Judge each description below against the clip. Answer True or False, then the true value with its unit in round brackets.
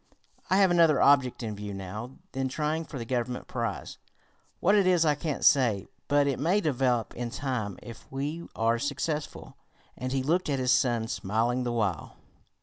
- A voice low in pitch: True (130 Hz)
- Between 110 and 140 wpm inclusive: False (180 wpm)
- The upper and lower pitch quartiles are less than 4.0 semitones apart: False (4.4 semitones)